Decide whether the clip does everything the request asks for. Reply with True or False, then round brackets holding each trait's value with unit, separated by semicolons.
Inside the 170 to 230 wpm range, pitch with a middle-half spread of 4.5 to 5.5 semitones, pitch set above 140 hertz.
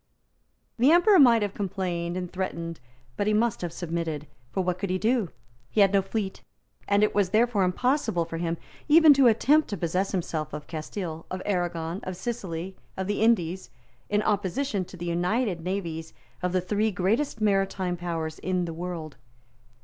False (175 wpm; 3.7 semitones; 185 Hz)